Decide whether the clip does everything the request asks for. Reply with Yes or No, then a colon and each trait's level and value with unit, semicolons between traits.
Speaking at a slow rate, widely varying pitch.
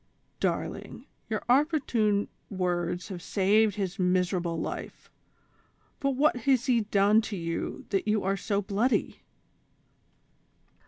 No: slow, 120 wpm; average, 3.8 semitones